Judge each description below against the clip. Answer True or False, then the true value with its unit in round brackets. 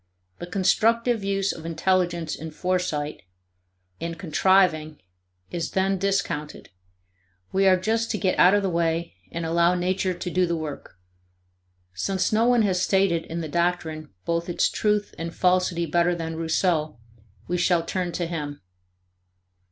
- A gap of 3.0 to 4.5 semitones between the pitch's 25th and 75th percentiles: False (2.5 semitones)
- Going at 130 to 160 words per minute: True (150 wpm)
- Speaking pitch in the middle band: True (175 Hz)